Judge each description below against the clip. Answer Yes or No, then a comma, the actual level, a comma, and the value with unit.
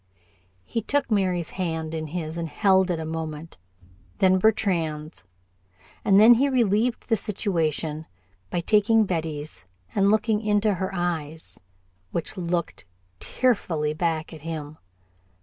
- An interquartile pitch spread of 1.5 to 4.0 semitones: No, average, 4.6 semitones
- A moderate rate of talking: No, slow, 130 wpm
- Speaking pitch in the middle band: Yes, medium, 175 Hz